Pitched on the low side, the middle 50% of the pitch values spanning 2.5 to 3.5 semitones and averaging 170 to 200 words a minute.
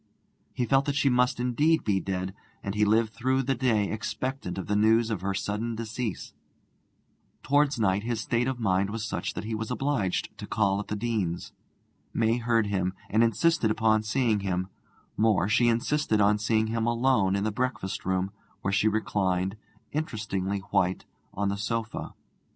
Yes: low, 110 Hz; average, 3.2 semitones; average, 175 wpm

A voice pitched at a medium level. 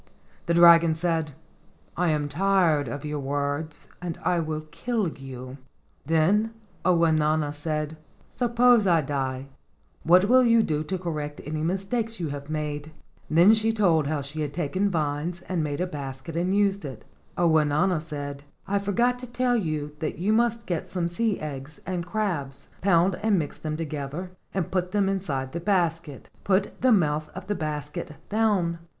Yes: medium, 165 Hz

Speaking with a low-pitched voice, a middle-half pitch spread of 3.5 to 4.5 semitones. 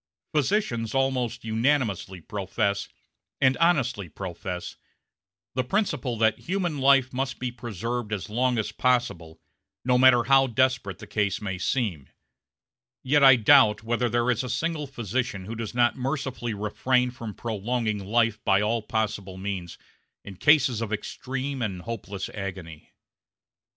Yes: low, 115 Hz; average, 4.1 semitones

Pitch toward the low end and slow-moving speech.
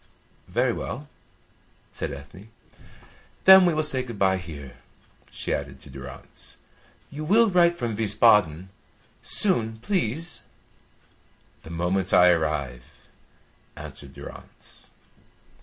Yes: low, 100 Hz; slow, 110 wpm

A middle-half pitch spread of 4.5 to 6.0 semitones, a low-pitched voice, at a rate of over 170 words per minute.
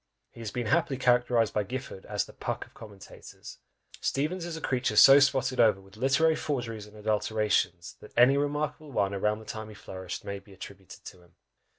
Yes: average, 4.9 semitones; low, 110 Hz; average, 195 wpm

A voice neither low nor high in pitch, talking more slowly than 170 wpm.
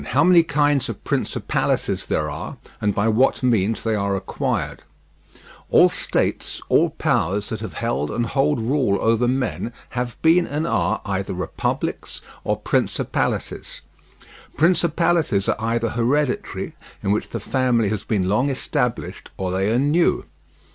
No: low, 115 Hz; average, 145 wpm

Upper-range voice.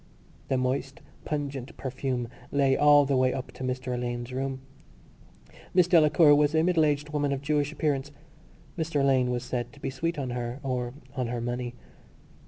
No: low, 135 Hz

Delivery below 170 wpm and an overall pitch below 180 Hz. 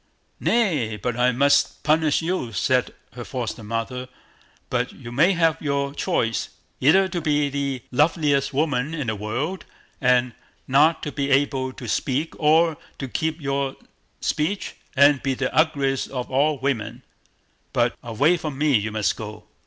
Yes: average, 155 wpm; medium, 140 Hz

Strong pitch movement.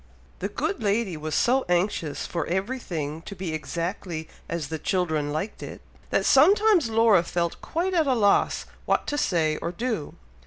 Yes: wide, 6.5 semitones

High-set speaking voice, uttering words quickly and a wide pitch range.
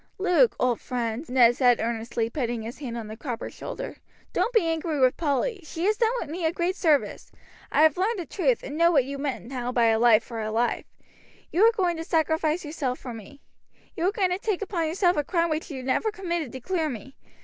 Yes: very high, 300 Hz; fast, 225 wpm; wide, 6.3 semitones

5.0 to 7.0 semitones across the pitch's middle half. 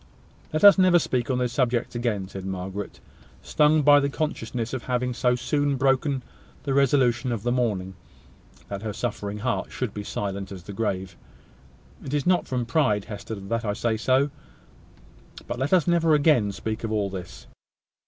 Yes: average, 5.3 semitones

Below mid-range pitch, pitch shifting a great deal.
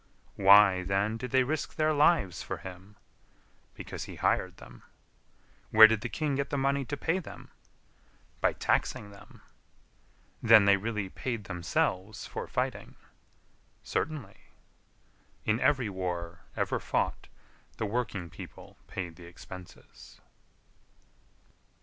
Yes: low, 105 Hz; wide, 6.0 semitones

